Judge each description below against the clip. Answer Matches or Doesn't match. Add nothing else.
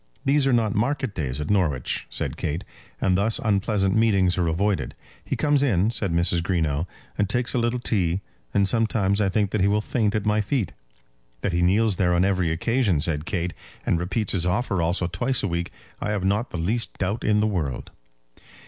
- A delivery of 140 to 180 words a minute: Doesn't match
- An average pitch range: Matches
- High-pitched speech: Doesn't match